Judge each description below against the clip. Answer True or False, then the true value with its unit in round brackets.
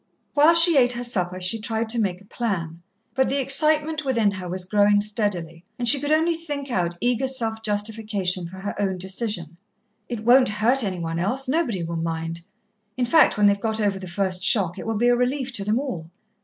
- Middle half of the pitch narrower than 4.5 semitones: False (5.5 semitones)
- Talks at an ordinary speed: False (210 wpm)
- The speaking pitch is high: True (215 Hz)